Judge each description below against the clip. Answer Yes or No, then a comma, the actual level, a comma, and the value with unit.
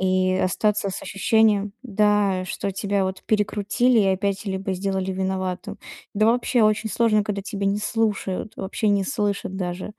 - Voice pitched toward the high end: Yes, high, 200 Hz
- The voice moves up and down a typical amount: No, narrow, 1.9 semitones